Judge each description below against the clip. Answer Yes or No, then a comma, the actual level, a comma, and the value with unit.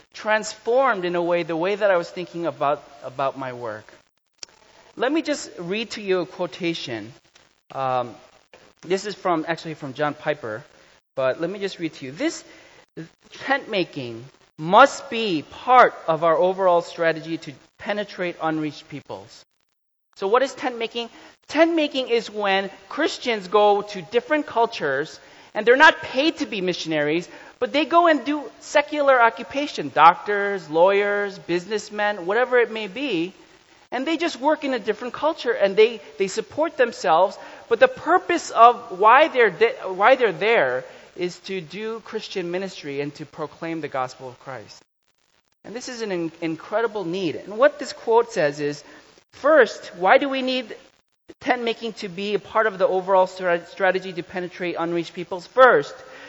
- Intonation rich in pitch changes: Yes, wide, 7.0 semitones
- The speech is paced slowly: No, average, 165 wpm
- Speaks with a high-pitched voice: Yes, high, 200 Hz